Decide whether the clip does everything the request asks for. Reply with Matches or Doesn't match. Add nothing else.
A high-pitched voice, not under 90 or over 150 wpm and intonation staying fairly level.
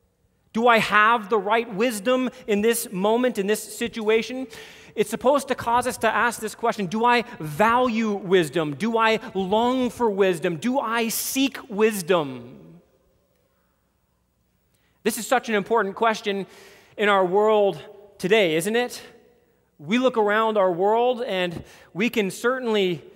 Doesn't match